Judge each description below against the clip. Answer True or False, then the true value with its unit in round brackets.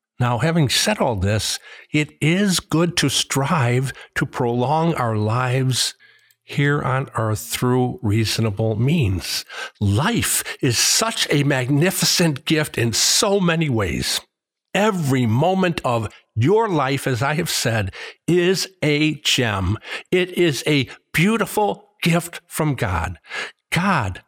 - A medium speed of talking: False (125 wpm)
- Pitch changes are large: True (6.4 semitones)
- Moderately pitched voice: True (145 Hz)